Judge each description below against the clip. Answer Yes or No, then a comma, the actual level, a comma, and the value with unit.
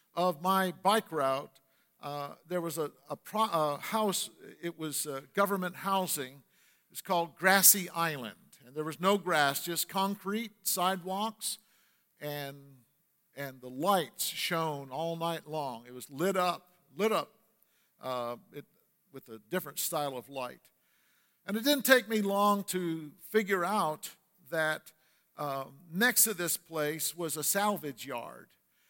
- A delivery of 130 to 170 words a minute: Yes, average, 145 wpm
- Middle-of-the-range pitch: Yes, medium, 170 Hz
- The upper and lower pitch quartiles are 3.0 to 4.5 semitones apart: No, average, 5.1 semitones